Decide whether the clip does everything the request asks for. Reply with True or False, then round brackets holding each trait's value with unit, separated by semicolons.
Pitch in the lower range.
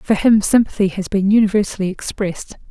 False (200 Hz)